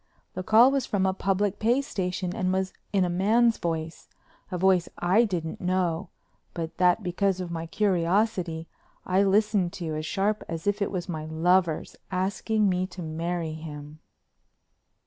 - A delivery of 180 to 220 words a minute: No, average, 160 wpm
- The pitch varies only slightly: No, average, 3.0 semitones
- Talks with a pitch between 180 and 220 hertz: Yes, medium, 185 Hz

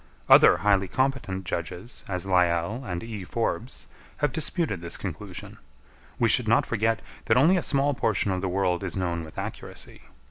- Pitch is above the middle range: No, low, 100 Hz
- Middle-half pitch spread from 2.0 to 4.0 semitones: No, average, 5.2 semitones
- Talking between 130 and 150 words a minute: No, average, 170 wpm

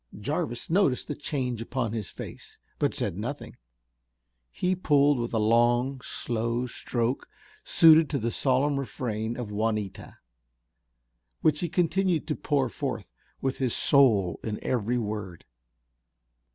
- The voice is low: Yes, low, 125 Hz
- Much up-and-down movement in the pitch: No, average, 4.2 semitones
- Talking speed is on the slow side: Yes, slow, 130 wpm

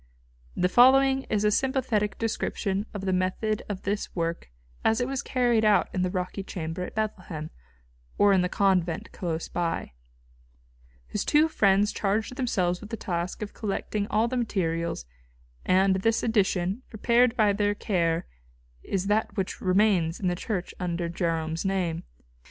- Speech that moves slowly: No, average, 155 wpm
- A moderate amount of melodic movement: Yes, average, 3.4 semitones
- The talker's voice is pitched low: No, high, 195 Hz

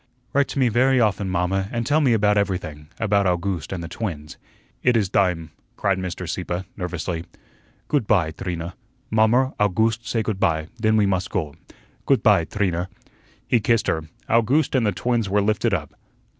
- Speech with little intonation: No, average, 4.3 semitones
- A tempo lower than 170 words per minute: No, average, 175 wpm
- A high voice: No, low, 100 Hz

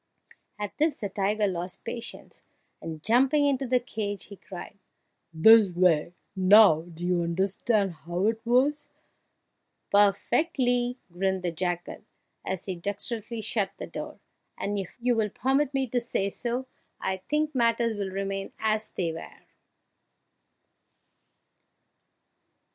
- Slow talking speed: Yes, slow, 125 wpm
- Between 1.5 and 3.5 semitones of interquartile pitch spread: No, average, 4.6 semitones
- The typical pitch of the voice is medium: No, high, 205 Hz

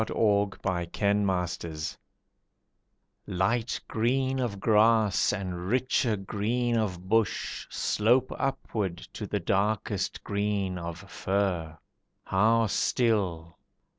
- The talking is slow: Yes, slow, 100 wpm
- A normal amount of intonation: Yes, average, 3.5 semitones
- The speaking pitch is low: Yes, low, 100 Hz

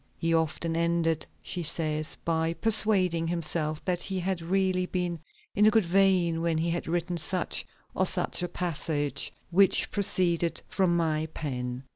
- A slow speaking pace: No, average, 155 wpm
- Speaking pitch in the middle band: Yes, medium, 170 Hz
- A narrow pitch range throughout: Yes, narrow, 2.1 semitones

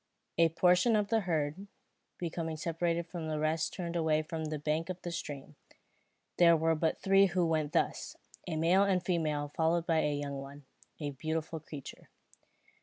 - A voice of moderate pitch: Yes, medium, 165 Hz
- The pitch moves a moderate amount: No, narrow, 2.2 semitones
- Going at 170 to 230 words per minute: Yes, average, 175 wpm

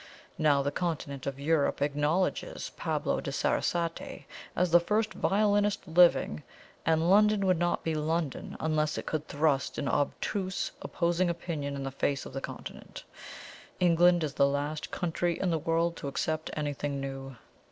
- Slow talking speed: No, average, 155 wpm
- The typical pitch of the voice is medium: Yes, medium, 160 Hz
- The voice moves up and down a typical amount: Yes, average, 3.5 semitones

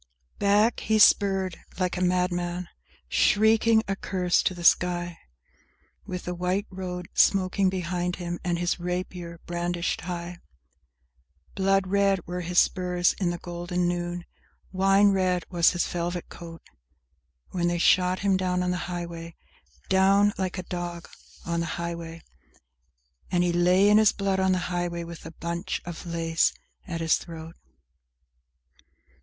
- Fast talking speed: No, average, 150 wpm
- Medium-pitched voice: Yes, medium, 180 Hz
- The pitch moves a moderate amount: No, narrow, 1.5 semitones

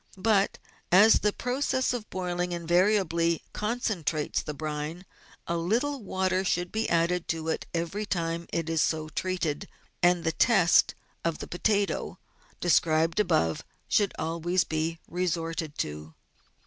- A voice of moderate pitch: Yes, medium, 175 Hz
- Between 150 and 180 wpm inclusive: No, slow, 135 wpm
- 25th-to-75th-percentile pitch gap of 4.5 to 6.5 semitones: No, average, 3.2 semitones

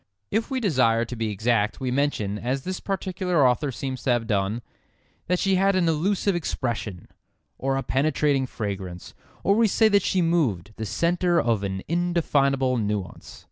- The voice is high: No, low, 135 Hz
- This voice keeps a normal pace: Yes, average, 170 wpm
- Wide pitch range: Yes, wide, 7.9 semitones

